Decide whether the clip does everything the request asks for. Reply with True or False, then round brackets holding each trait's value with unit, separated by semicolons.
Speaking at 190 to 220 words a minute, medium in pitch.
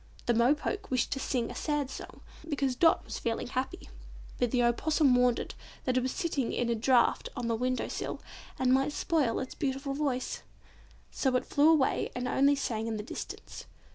False (200 wpm; 260 Hz)